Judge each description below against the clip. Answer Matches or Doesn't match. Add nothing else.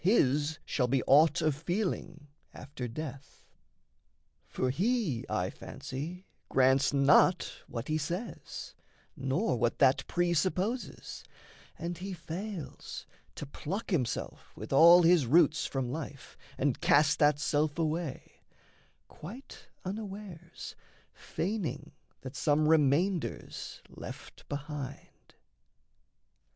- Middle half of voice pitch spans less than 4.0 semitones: Doesn't match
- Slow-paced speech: Matches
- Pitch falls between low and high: Matches